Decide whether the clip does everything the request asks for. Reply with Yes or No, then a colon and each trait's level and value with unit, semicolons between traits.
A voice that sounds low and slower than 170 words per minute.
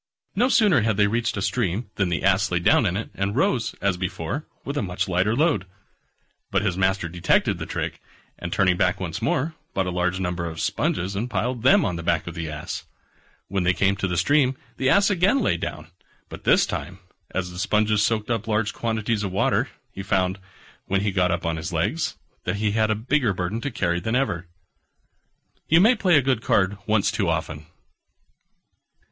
No: low, 100 Hz; fast, 205 wpm